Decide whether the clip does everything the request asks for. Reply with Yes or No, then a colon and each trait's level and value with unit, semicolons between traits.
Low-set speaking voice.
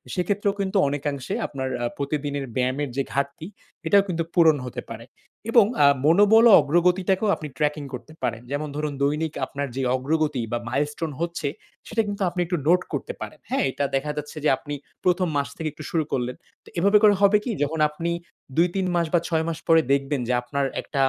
No: medium, 155 Hz